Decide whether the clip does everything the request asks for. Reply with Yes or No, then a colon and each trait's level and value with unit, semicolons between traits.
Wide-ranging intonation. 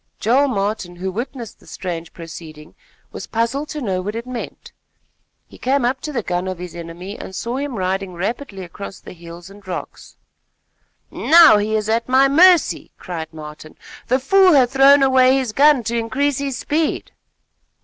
Yes: wide, 6.7 semitones